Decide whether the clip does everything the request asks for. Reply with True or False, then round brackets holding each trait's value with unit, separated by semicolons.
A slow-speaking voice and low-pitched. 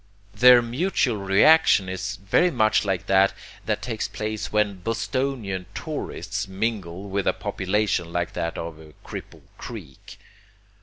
True (125 wpm; 100 Hz)